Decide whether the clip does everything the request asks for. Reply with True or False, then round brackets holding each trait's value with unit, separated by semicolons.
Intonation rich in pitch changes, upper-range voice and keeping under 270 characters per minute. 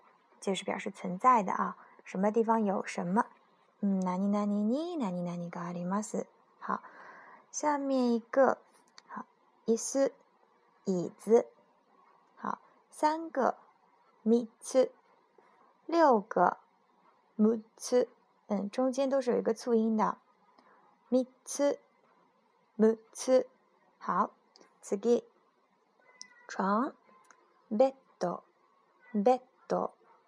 True (5.8 semitones; 240 Hz; 160 characters per minute)